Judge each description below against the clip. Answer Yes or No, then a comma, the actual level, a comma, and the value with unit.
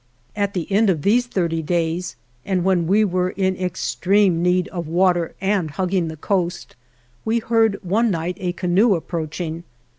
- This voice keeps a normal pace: Yes, average, 170 wpm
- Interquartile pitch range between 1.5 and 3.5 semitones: Yes, average, 2.7 semitones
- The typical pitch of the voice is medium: Yes, medium, 180 Hz